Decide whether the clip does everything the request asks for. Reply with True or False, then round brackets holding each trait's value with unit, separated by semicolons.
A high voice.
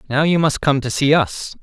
False (140 Hz)